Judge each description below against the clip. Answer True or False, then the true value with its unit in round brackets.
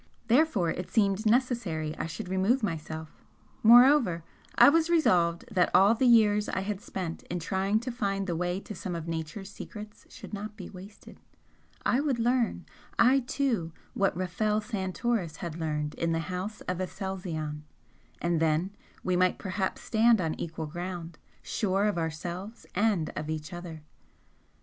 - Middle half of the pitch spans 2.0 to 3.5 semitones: False (4.4 semitones)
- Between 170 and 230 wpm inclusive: False (160 wpm)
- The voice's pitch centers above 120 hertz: True (190 Hz)